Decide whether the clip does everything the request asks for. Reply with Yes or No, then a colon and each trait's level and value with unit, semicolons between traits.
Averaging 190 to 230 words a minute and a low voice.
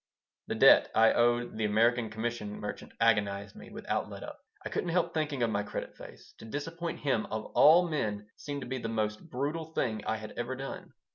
Yes: fast, 205 wpm; low, 120 Hz